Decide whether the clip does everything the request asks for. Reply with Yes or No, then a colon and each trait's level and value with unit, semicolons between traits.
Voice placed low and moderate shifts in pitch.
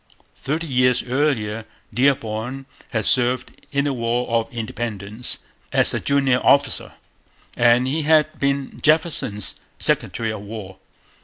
Yes: low, 125 Hz; average, 3.8 semitones